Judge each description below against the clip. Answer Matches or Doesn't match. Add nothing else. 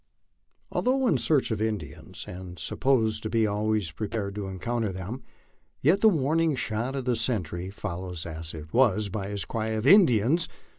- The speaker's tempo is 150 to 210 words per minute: Matches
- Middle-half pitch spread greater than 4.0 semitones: Matches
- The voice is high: Doesn't match